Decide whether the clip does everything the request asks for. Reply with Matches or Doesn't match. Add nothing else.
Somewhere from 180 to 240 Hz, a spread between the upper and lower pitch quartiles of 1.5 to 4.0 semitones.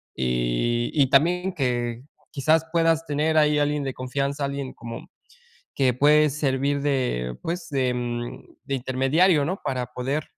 Doesn't match